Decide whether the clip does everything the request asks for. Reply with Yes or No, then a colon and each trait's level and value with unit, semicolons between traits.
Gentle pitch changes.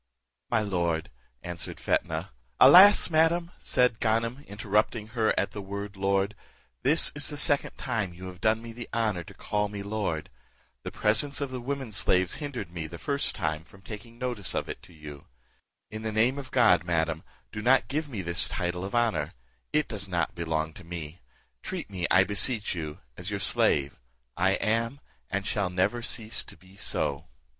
No: average, 5.1 semitones